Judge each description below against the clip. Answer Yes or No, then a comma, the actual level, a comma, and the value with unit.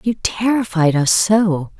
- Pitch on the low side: No, high, 190 Hz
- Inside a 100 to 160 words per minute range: Yes, slow, 135 wpm